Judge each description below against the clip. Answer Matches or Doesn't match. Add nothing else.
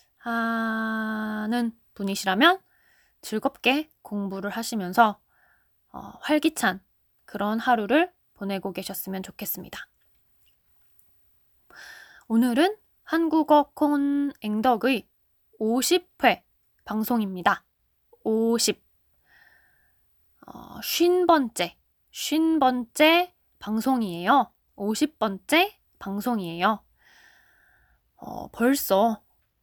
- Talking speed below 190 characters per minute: Matches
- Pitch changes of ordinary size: Doesn't match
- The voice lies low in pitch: Doesn't match